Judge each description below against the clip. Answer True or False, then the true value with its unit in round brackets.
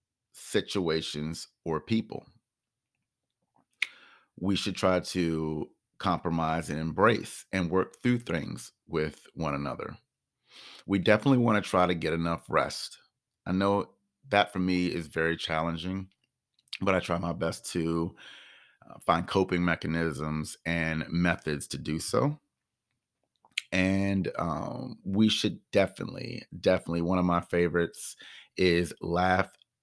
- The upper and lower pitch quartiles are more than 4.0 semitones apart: False (2.9 semitones)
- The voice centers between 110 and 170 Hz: False (90 Hz)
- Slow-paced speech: True (120 wpm)